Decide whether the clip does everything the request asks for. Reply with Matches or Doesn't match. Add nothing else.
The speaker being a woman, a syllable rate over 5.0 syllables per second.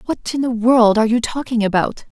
Matches